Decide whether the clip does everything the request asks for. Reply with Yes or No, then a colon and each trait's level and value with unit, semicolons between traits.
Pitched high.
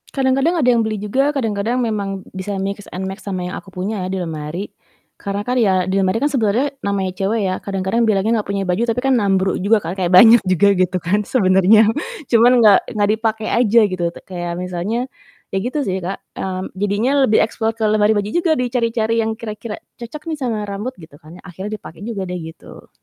Yes: high, 205 Hz